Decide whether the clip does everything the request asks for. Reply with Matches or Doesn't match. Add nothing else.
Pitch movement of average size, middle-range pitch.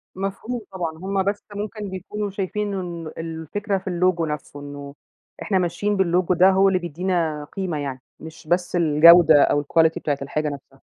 Matches